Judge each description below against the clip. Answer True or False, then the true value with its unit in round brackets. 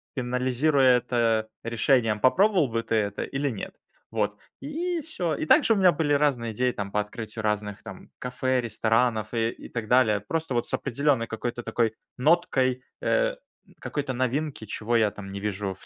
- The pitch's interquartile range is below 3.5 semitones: False (4.4 semitones)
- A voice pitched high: False (120 Hz)